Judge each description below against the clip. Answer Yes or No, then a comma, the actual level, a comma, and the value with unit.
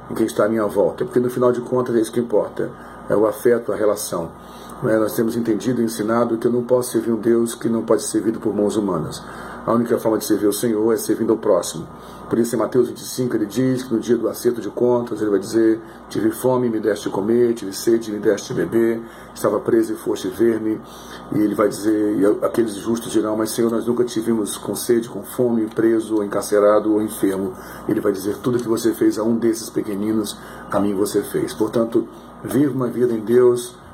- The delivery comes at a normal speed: No, fast, 230 wpm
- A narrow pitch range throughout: Yes, narrow, 2.0 semitones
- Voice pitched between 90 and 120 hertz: Yes, low, 115 Hz